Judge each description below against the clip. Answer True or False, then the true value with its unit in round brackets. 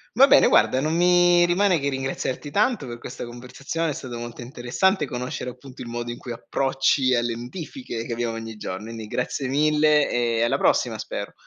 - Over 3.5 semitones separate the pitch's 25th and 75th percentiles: True (4.3 semitones)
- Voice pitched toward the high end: False (130 Hz)